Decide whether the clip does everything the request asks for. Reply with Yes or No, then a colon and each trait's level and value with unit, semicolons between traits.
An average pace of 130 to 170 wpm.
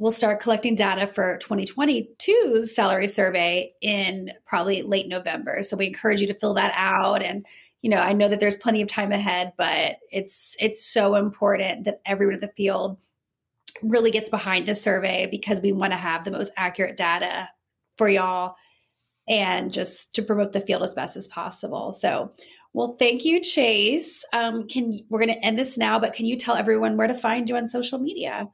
No: average, 195 wpm